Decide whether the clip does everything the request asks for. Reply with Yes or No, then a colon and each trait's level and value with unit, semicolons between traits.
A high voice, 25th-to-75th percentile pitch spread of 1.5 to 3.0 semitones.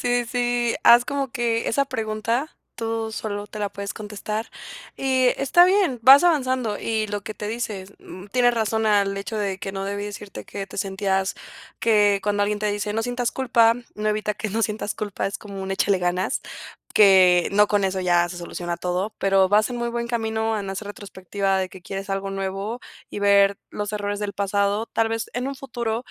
Yes: high, 210 Hz; average, 2.7 semitones